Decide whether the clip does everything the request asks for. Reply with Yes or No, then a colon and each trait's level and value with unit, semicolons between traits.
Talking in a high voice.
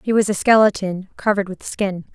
Yes: high, 195 Hz